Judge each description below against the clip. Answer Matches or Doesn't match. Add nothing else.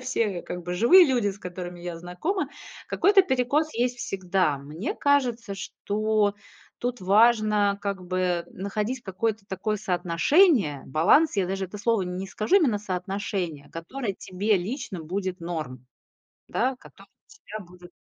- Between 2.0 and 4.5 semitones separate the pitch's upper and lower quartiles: Doesn't match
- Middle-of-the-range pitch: Doesn't match